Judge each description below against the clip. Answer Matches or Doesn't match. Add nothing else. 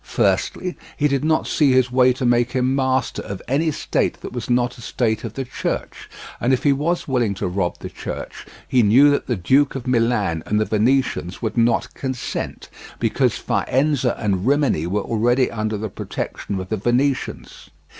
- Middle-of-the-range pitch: Doesn't match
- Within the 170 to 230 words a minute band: Matches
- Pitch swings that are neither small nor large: Matches